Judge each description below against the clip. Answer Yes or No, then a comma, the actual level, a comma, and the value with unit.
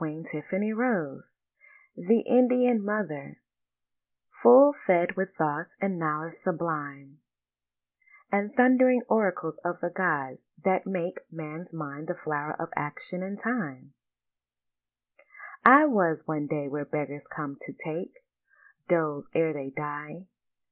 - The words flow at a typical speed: No, slow, 115 wpm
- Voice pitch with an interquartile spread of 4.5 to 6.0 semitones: Yes, wide, 5.5 semitones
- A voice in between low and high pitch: Yes, medium, 170 Hz